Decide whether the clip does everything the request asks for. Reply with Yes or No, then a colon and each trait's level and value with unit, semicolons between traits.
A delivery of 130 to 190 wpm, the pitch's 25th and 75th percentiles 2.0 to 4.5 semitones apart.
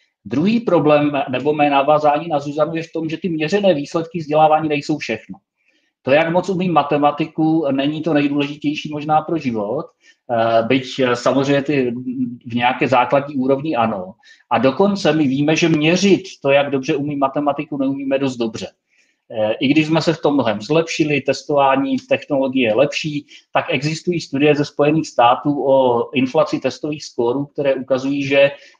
Yes: average, 155 wpm; narrow, 2.6 semitones